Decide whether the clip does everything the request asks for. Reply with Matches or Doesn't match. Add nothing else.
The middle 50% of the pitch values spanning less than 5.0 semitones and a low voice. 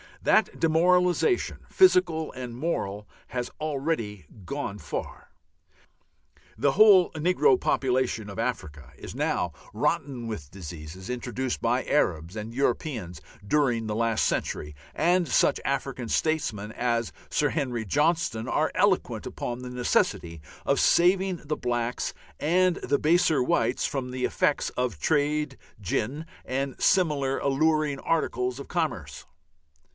Doesn't match